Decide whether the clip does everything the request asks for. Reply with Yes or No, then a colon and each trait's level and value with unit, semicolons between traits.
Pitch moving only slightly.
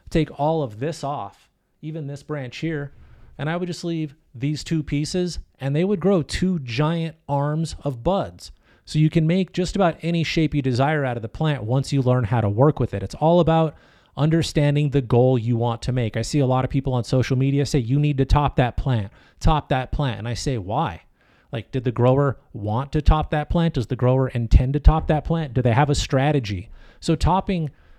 No: average, 3.8 semitones